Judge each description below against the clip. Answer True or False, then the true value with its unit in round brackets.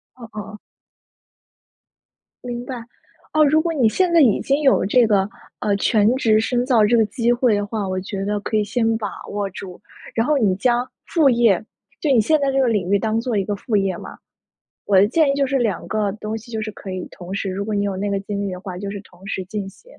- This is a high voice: True (215 Hz)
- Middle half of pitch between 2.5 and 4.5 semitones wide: True (3.6 semitones)